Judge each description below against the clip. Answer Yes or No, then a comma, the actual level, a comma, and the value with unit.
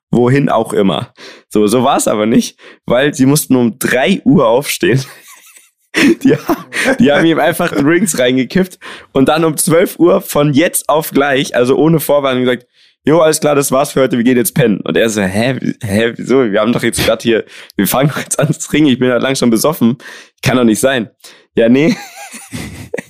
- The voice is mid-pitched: No, low, 130 Hz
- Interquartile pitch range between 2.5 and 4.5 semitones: Yes, average, 3.2 semitones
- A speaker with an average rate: No, fast, 200 wpm